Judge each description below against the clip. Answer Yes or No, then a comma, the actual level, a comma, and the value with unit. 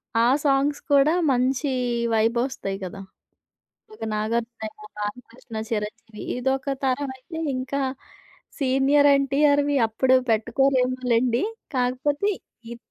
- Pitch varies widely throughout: No, average, 3.2 semitones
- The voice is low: No, very high, 255 Hz